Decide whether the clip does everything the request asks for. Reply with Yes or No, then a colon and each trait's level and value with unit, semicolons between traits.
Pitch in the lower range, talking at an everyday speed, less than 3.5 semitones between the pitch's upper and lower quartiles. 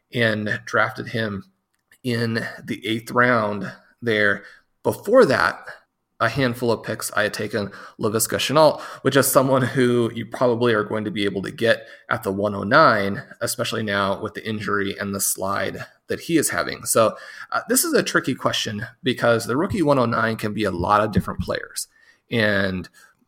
Yes: low, 110 Hz; average, 170 wpm; average, 2.7 semitones